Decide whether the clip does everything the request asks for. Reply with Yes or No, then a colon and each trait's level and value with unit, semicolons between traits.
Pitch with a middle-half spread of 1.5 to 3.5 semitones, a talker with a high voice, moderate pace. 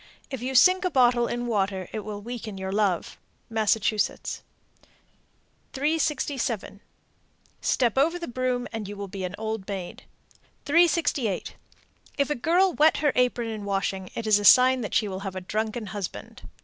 No: average, 4.5 semitones; high, 225 Hz; average, 160 wpm